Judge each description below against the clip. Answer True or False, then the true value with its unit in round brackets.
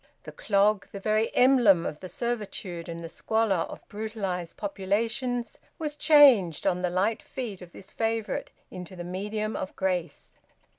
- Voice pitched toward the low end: False (205 Hz)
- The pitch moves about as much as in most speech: True (3.8 semitones)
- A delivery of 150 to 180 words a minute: True (155 wpm)